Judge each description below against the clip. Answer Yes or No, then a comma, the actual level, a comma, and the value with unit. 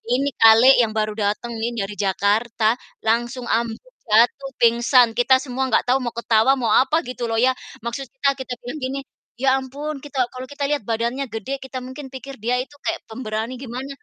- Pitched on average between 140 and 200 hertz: No, high, 245 Hz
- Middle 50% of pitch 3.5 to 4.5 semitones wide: No, average, 2.8 semitones